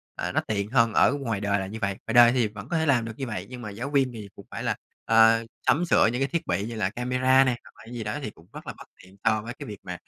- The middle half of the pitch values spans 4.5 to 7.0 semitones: No, average, 3.5 semitones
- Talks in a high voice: No, low, 115 Hz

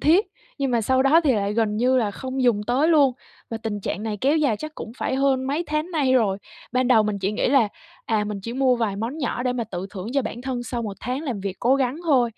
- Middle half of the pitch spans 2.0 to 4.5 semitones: Yes, average, 3.9 semitones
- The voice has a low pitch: No, high, 245 Hz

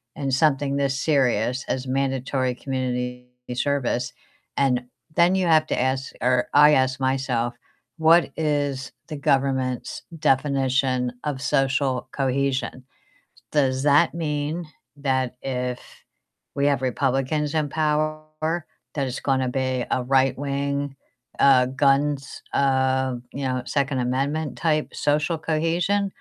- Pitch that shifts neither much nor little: No, narrow, 2.2 semitones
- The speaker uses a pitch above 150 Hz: No, low, 135 Hz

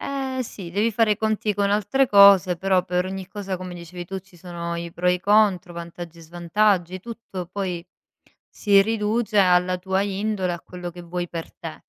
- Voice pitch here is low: No, medium, 185 Hz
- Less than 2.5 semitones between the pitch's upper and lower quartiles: No, average, 2.8 semitones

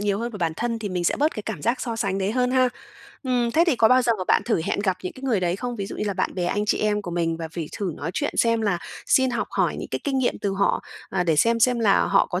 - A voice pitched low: No, high, 215 Hz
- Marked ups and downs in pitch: No, average, 4.7 semitones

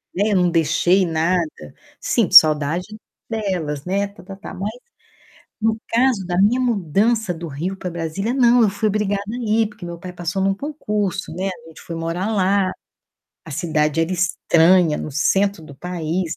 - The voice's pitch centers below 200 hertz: Yes, medium, 185 Hz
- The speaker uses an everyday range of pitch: Yes, average, 3.7 semitones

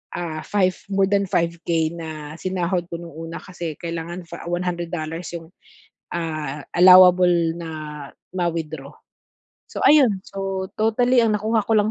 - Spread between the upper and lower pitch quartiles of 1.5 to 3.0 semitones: Yes, narrow, 2.6 semitones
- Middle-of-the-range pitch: Yes, medium, 175 Hz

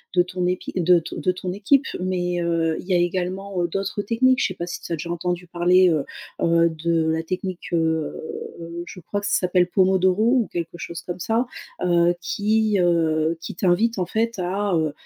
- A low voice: No, medium, 180 Hz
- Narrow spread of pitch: Yes, narrow, 2.3 semitones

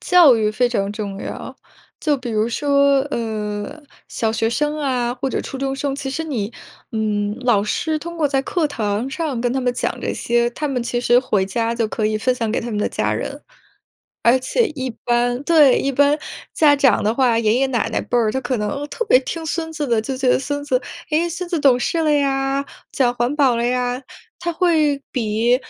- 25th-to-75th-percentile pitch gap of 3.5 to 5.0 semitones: Yes, average, 3.8 semitones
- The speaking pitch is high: Yes, very high, 255 Hz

